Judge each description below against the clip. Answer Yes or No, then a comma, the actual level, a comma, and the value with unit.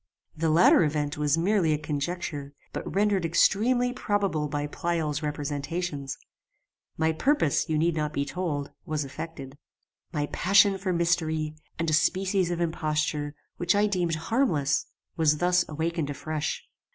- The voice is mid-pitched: Yes, medium, 160 Hz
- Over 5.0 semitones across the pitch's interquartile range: No, average, 3.2 semitones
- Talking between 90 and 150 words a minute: Yes, average, 140 wpm